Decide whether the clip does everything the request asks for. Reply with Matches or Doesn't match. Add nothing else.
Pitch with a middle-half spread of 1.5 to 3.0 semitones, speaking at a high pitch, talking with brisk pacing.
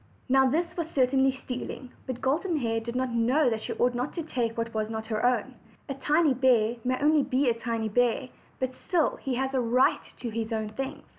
Matches